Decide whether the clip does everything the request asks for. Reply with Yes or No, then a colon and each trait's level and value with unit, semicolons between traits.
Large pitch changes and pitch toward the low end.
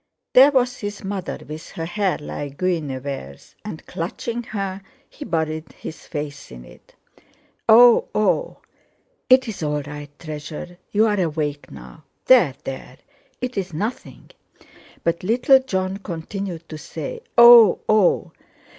No: wide, 6.2 semitones; medium, 180 Hz